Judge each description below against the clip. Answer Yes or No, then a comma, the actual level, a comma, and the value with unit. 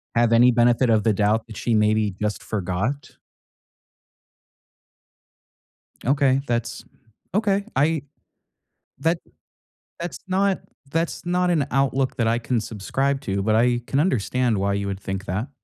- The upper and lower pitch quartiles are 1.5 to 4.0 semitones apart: No, average, 4.7 semitones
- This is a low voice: Yes, low, 120 Hz